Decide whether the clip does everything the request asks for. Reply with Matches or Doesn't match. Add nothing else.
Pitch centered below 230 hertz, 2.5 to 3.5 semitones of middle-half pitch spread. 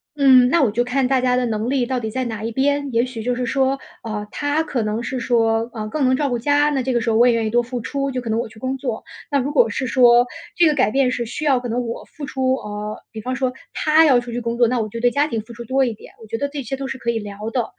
Doesn't match